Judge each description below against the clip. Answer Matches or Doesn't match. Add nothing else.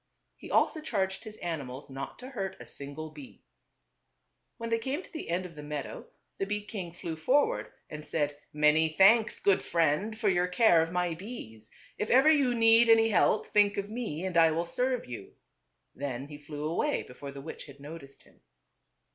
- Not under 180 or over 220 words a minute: Matches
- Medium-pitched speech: Matches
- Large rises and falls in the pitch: Matches